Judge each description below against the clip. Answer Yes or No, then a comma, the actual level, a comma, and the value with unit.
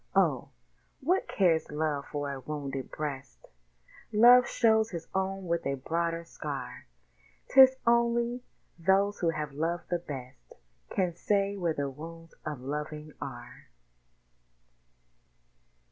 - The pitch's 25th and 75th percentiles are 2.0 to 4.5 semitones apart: No, wide, 5.4 semitones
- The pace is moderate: No, slow, 120 wpm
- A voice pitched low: No, medium, 165 Hz